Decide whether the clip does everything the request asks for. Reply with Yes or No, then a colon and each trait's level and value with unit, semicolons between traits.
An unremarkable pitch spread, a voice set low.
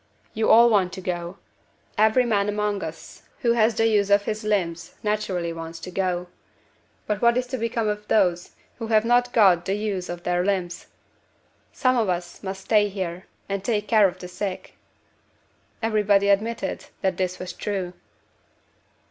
No: average, 3.1 semitones; high, 200 Hz